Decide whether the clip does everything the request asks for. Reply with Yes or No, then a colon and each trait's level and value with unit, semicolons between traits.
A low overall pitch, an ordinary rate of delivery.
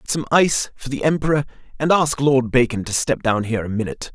No: low, 130 Hz; fast, 230 wpm